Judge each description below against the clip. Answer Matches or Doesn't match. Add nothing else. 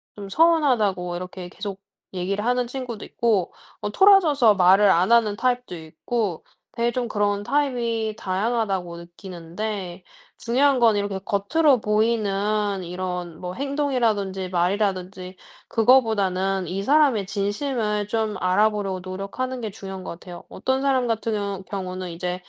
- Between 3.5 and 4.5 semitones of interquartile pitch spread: Matches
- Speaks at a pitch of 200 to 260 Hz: Matches